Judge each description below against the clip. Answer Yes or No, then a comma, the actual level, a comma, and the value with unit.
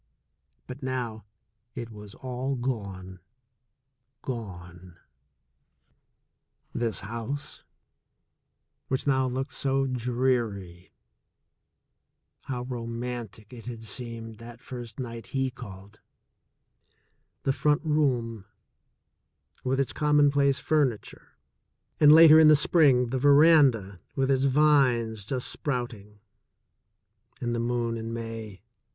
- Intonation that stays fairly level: No, average, 3.2 semitones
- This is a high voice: No, low, 125 Hz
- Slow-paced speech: Yes, slow, 105 wpm